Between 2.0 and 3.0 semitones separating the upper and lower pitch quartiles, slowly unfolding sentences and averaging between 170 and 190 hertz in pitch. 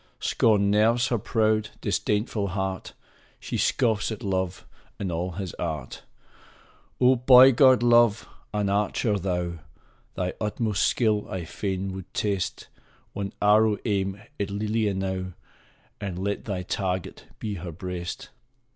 No: narrow, 2.6 semitones; slow, 130 wpm; low, 100 Hz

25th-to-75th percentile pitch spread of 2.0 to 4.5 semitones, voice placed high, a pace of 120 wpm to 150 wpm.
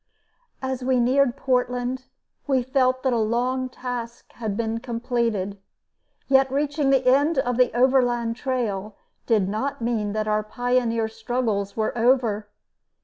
Yes: narrow, 2.5 semitones; high, 245 Hz; average, 140 wpm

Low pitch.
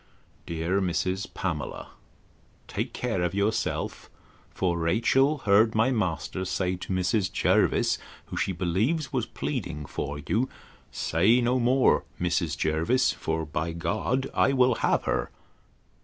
Yes: very low, 95 Hz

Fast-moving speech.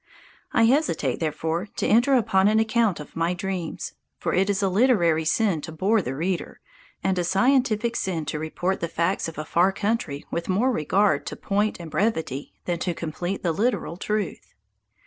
No: average, 185 wpm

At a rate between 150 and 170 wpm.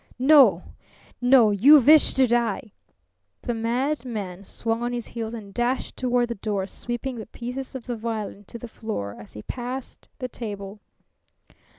Yes: average, 160 wpm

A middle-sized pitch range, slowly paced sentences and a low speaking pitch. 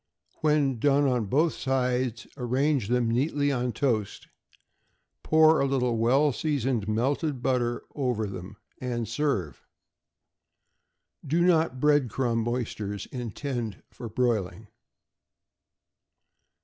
Yes: average, 3.7 semitones; slow, 105 wpm; low, 125 Hz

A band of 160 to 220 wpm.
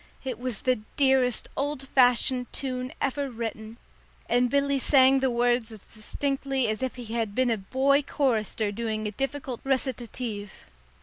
No: average, 150 wpm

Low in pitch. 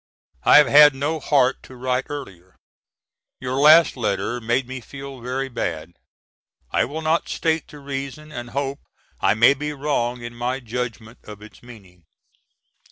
Yes: low, 130 Hz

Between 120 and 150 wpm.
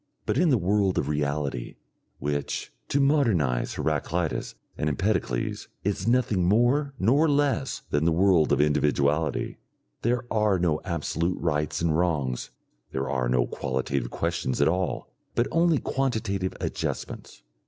Yes: slow, 135 wpm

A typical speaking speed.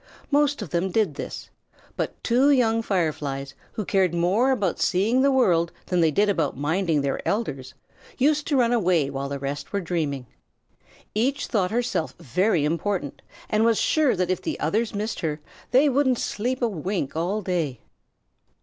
Yes: average, 170 wpm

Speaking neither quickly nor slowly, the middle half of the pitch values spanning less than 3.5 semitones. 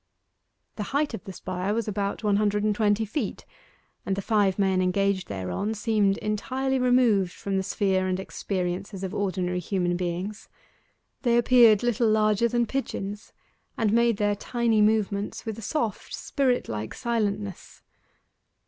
Yes: average, 150 wpm; average, 2.9 semitones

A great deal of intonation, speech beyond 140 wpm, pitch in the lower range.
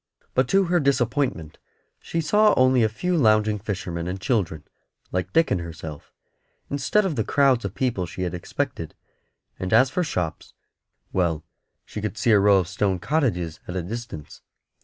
Yes: wide, 7.0 semitones; average, 170 wpm; low, 110 Hz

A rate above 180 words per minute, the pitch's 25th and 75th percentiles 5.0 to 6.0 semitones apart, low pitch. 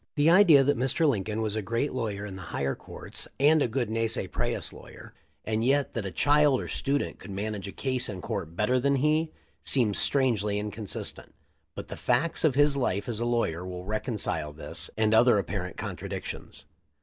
Yes: average, 195 wpm; average, 5.3 semitones; low, 115 Hz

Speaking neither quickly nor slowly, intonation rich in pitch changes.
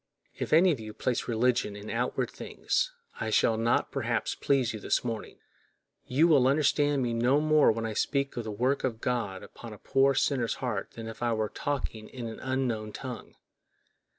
No: average, 190 wpm; average, 3.3 semitones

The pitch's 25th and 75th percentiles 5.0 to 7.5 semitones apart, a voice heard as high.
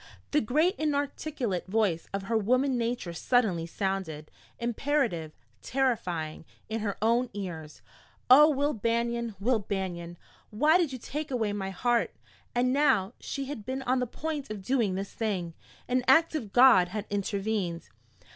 Yes: wide, 5.4 semitones; high, 230 Hz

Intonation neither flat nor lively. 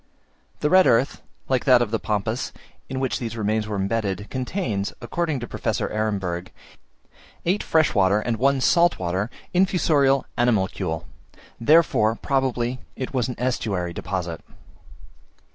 Yes: average, 4.9 semitones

